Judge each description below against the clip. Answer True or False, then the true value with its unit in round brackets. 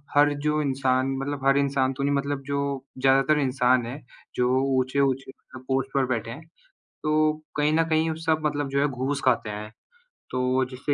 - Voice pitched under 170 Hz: True (135 Hz)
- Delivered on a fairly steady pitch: True (2.0 semitones)